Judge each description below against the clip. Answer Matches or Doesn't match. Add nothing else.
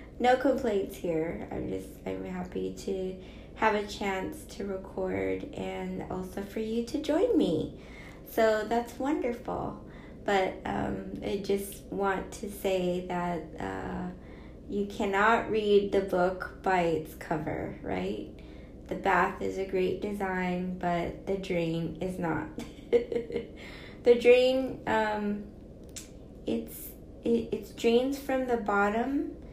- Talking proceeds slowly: Matches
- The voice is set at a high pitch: Matches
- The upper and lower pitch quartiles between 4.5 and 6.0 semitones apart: Matches